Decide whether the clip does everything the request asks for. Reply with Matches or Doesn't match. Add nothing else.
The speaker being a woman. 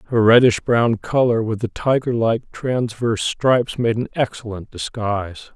Doesn't match